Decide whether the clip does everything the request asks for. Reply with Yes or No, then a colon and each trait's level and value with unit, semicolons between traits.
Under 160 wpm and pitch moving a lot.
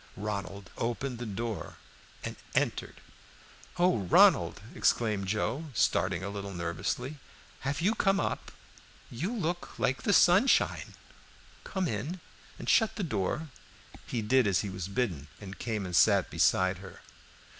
Yes: average, 140 wpm; wide, 8.2 semitones